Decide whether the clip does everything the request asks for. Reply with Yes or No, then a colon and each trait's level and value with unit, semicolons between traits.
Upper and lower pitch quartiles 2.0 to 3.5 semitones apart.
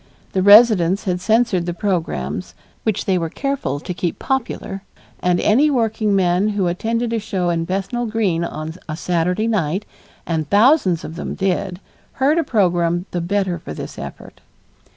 No: average, 4.1 semitones